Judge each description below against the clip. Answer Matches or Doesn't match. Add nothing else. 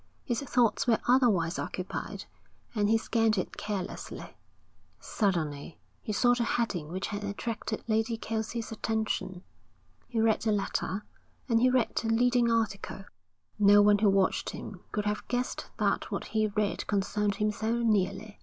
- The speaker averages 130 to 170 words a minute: Matches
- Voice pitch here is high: Matches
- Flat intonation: Matches